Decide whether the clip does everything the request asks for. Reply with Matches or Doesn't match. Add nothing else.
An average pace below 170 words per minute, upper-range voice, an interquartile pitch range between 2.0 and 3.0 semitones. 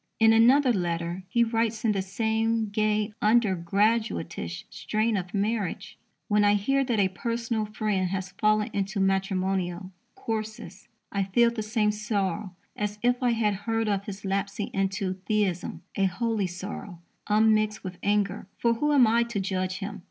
Matches